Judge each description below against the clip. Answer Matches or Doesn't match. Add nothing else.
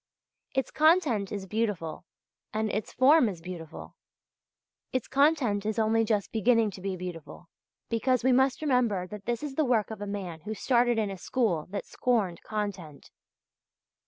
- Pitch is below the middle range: Doesn't match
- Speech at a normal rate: Matches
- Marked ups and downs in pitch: Doesn't match